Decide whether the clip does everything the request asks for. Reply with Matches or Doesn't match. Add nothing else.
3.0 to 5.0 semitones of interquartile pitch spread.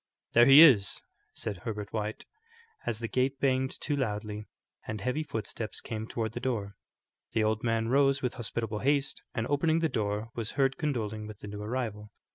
Matches